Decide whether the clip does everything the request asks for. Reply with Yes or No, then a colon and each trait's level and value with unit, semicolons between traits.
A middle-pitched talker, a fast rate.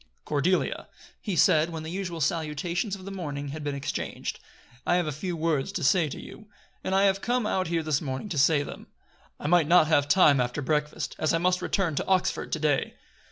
Yes: medium, 160 Hz; fast, 215 wpm